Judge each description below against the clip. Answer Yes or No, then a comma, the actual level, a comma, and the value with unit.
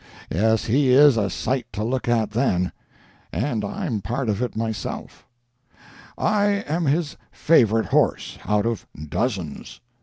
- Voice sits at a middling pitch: No, low, 115 Hz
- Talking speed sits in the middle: No, slow, 130 wpm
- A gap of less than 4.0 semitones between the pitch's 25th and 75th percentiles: No, average, 4.4 semitones